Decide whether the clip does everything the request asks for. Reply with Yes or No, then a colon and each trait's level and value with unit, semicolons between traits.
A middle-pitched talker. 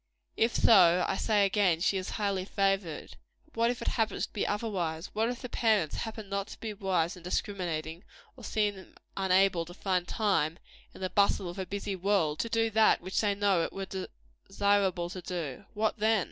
No: high, 195 Hz